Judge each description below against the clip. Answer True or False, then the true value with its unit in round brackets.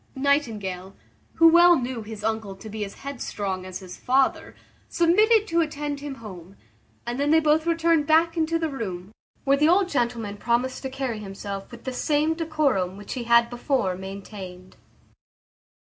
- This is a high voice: True (250 Hz)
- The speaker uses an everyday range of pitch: False (7.2 semitones)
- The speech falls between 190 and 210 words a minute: False (165 wpm)